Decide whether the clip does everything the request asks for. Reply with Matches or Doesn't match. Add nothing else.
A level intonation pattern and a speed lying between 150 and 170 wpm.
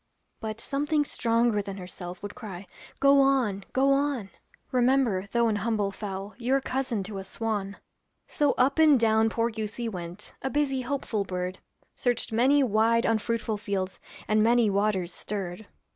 Doesn't match